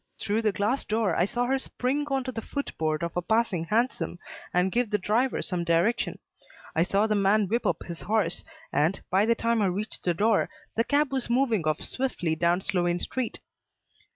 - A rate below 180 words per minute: No, fast, 205 wpm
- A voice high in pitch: Yes, high, 210 Hz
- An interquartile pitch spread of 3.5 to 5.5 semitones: Yes, average, 5.1 semitones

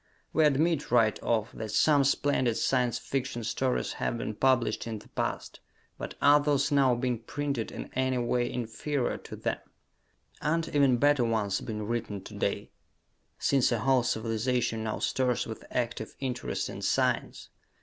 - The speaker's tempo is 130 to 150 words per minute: No, average, 160 wpm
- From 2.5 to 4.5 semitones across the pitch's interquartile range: Yes, average, 3.3 semitones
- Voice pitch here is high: No, low, 125 Hz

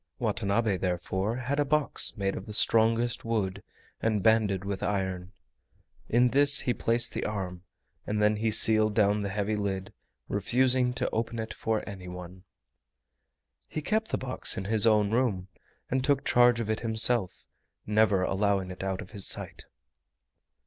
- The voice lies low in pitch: Yes, low, 105 Hz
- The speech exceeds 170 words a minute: No, average, 160 wpm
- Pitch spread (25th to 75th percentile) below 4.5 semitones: Yes, average, 3.2 semitones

